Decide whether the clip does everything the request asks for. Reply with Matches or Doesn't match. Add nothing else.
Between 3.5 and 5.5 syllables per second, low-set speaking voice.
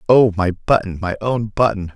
Matches